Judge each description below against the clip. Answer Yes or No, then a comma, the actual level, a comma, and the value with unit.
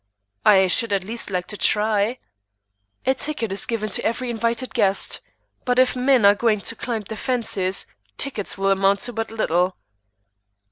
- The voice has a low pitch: No, high, 220 Hz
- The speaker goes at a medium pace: Yes, average, 170 wpm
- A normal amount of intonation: Yes, average, 3.4 semitones